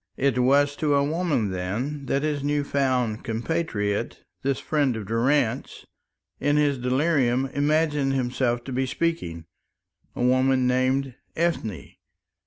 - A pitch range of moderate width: Yes, average, 3.0 semitones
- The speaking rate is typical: No, slow, 130 wpm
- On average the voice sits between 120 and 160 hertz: Yes, low, 135 Hz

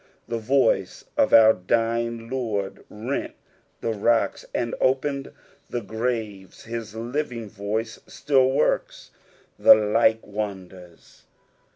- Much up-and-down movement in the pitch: No, narrow, 2.5 semitones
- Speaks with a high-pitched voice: No, low, 115 Hz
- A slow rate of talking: Yes, slow, 105 wpm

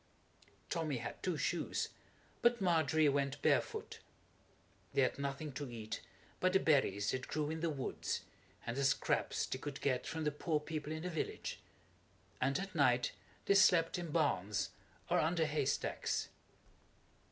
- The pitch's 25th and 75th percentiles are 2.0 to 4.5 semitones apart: Yes, average, 3.4 semitones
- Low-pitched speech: No, medium, 150 Hz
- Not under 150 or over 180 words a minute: Yes, average, 155 wpm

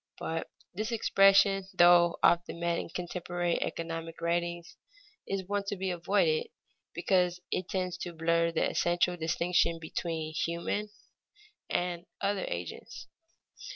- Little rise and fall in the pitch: Yes, narrow, 2.2 semitones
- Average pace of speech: No, slow, 120 wpm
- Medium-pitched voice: Yes, medium, 175 Hz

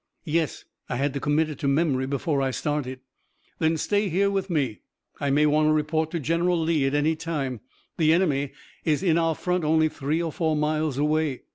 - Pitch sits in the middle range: Yes, medium, 155 Hz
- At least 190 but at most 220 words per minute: Yes, fast, 205 wpm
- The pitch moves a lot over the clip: No, narrow, 2.5 semitones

